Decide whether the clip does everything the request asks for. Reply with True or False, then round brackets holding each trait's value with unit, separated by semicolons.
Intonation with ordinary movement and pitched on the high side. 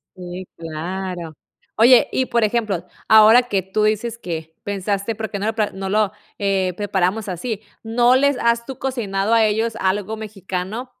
True (3.2 semitones; 210 Hz)